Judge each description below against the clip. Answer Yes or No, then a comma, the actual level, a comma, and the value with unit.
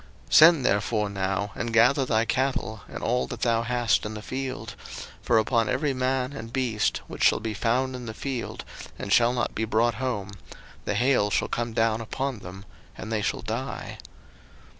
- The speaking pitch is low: Yes, low, 115 Hz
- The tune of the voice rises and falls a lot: No, average, 2.9 semitones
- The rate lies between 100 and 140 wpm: No, average, 185 wpm